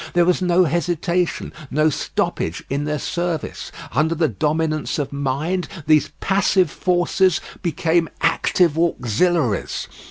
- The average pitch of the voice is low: No, medium, 165 Hz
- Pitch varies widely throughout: No, average, 2.8 semitones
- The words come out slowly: Yes, slow, 120 wpm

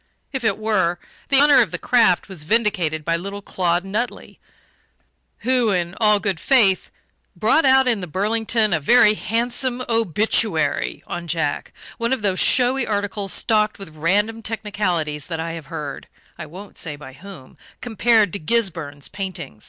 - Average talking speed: Yes, average, 160 wpm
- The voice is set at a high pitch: Yes, high, 200 Hz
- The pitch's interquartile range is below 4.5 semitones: No, average, 5.2 semitones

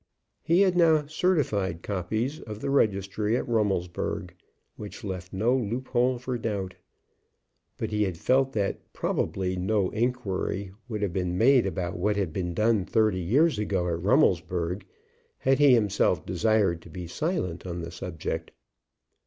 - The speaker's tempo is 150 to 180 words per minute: Yes, average, 155 wpm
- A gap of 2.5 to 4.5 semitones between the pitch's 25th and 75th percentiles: No, average, 5.1 semitones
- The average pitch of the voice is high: No, low, 105 Hz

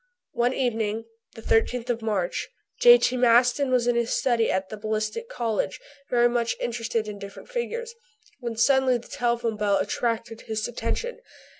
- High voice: Yes, high, 235 Hz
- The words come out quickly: No, average, 155 wpm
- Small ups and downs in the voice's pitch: Yes, narrow, 2.1 semitones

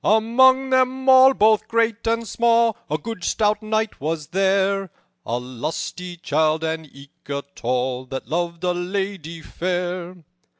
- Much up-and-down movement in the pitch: Yes, wide, 6.0 semitones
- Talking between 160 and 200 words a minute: No, average, 140 wpm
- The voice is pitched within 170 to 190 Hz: Yes, medium, 185 Hz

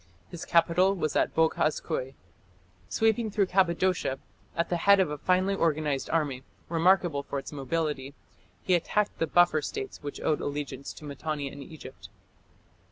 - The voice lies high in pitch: No, medium, 160 Hz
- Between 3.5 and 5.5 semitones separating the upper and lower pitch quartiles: Yes, average, 4.2 semitones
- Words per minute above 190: No, average, 155 wpm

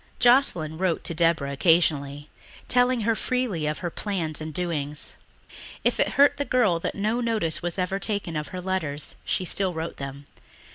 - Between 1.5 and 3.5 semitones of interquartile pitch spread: No, average, 5.2 semitones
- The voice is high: No, medium, 175 Hz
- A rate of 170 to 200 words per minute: Yes, average, 175 wpm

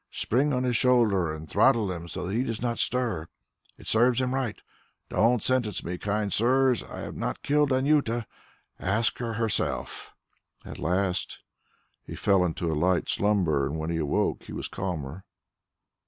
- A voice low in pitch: Yes, low, 105 Hz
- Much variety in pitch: Yes, wide, 5.9 semitones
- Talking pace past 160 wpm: Yes, average, 170 wpm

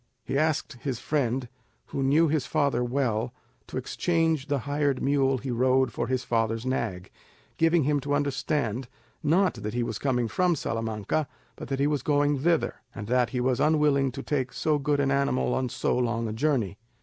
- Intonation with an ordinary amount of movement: Yes, average, 3.2 semitones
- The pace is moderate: Yes, average, 185 wpm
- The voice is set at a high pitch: No, low, 135 Hz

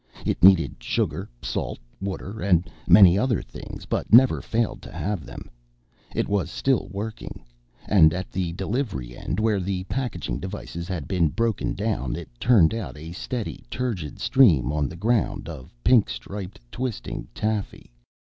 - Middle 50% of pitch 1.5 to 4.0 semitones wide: No, average, 4.7 semitones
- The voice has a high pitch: No, very low, 95 Hz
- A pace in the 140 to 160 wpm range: Yes, average, 155 wpm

